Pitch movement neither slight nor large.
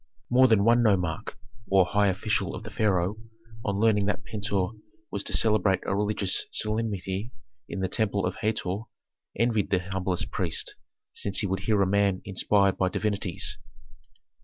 No: narrow, 2.2 semitones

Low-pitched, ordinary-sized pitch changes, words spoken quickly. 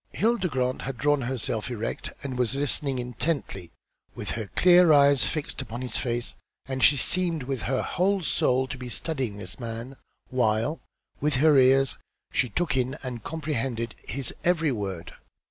No: low, 130 Hz; average, 3.8 semitones; average, 165 wpm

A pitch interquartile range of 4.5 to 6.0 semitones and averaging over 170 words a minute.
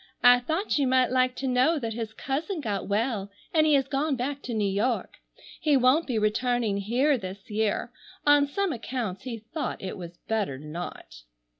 Yes: average, 4.8 semitones; average, 185 wpm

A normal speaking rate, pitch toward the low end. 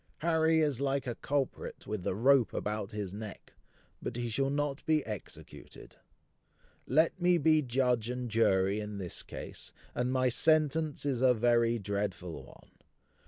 Yes: average, 155 wpm; low, 125 Hz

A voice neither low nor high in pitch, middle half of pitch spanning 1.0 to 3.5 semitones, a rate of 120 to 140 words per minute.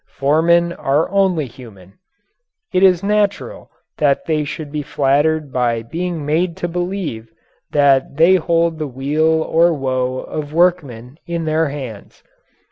No: medium, 155 Hz; average, 4.0 semitones; slow, 135 wpm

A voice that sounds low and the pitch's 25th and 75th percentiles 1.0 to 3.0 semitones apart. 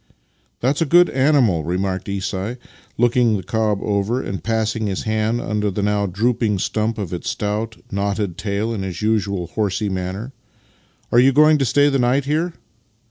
No: low, 110 Hz; average, 3.6 semitones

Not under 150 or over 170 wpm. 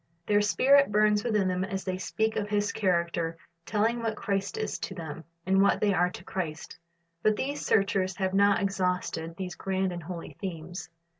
No: average, 180 wpm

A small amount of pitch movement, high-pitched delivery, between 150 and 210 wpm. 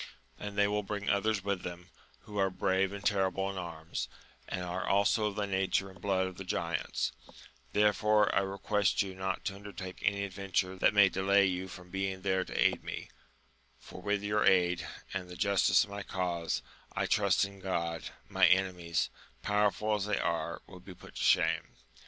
No: narrow, 1.8 semitones; very low, 95 Hz; average, 195 wpm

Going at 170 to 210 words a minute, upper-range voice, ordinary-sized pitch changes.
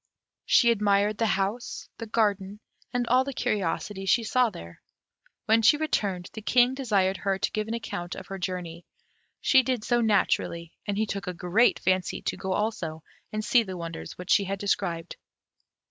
Yes: average, 175 wpm; high, 205 Hz; average, 3.5 semitones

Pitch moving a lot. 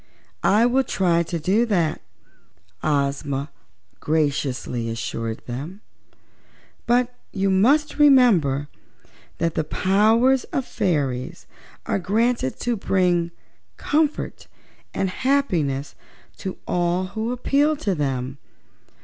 Yes: wide, 8.8 semitones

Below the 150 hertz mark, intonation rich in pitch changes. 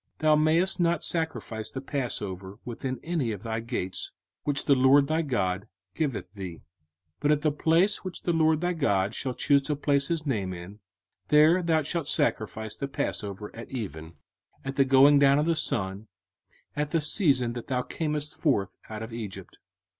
Yes: low, 135 Hz; wide, 6.0 semitones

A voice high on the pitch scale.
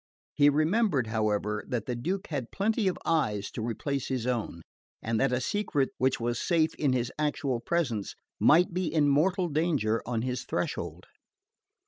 No: low, 135 Hz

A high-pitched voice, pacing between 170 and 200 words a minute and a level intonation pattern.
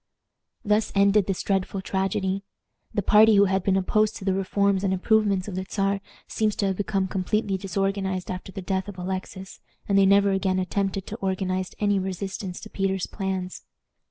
Yes: high, 195 Hz; average, 180 wpm; narrow, 1.1 semitones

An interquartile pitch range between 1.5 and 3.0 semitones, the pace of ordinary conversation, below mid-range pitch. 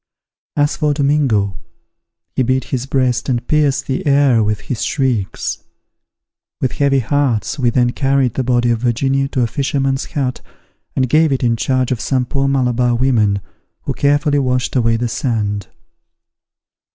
Yes: narrow, 2.5 semitones; average, 155 wpm; low, 130 Hz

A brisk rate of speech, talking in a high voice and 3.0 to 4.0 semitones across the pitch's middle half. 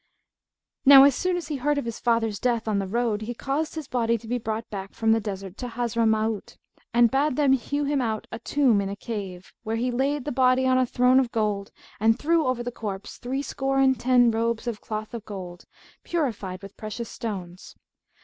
Yes: fast, 210 wpm; high, 235 Hz; average, 3.5 semitones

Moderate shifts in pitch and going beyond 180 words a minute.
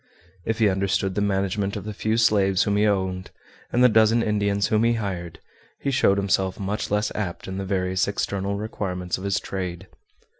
No: narrow, 2.0 semitones; average, 190 wpm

